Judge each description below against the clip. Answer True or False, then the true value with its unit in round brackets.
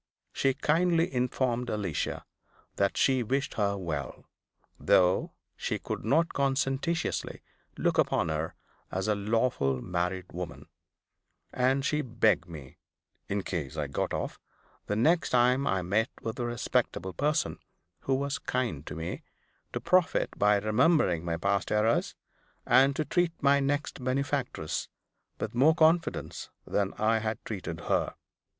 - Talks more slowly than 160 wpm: True (140 wpm)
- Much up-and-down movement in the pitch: True (6.8 semitones)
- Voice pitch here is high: False (115 Hz)